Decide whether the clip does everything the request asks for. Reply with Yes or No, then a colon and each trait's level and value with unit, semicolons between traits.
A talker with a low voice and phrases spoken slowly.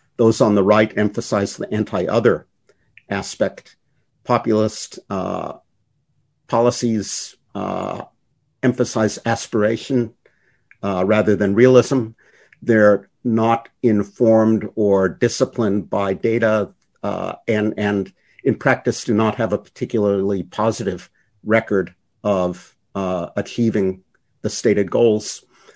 Yes: low, 110 Hz; slow, 100 wpm